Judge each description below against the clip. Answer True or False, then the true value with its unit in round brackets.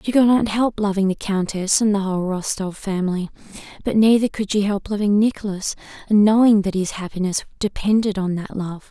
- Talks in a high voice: True (200 Hz)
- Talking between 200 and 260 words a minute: False (190 wpm)